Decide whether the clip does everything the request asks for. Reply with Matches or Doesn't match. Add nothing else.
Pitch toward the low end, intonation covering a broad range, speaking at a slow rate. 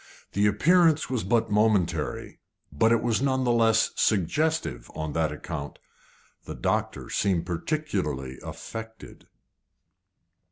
Matches